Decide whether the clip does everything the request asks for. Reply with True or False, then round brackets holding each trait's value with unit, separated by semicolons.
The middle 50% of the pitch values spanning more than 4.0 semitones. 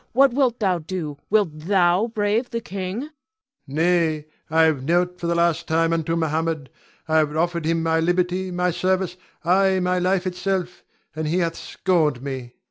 False (2.6 semitones)